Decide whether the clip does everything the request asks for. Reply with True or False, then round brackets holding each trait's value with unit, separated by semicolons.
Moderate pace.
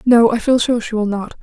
False (295 wpm)